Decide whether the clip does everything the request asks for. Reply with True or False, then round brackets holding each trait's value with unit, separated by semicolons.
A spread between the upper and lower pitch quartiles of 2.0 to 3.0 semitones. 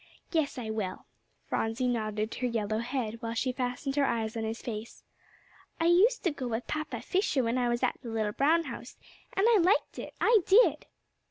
False (5.5 semitones)